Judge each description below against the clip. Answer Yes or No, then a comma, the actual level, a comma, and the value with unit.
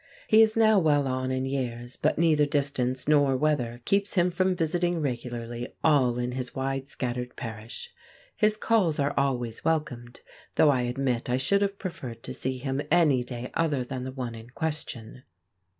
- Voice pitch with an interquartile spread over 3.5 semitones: Yes, average, 4.5 semitones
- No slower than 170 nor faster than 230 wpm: Yes, average, 175 wpm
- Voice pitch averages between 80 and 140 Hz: Yes, low, 135 Hz